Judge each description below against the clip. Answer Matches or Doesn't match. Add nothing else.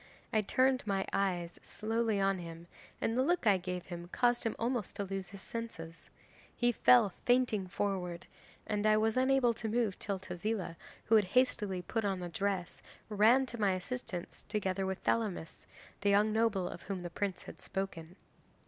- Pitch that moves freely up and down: Doesn't match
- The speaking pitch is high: Matches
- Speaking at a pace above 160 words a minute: Matches